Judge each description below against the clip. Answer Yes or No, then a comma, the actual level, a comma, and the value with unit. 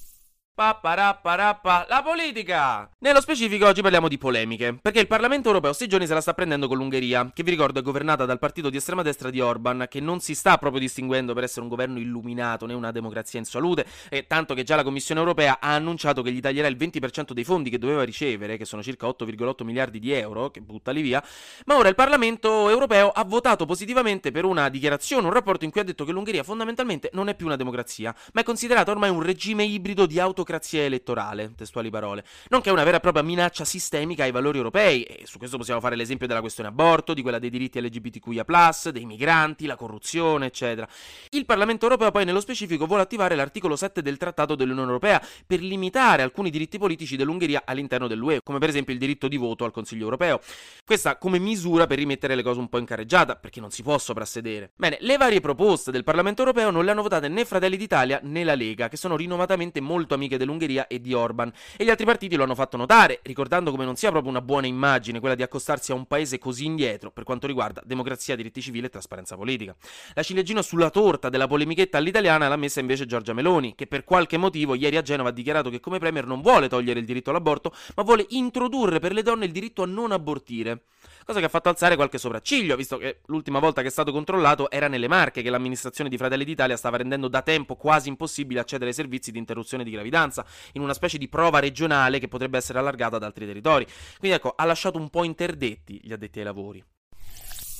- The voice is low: No, medium, 145 Hz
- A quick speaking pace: Yes, fast, 220 wpm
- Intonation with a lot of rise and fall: Yes, wide, 6.1 semitones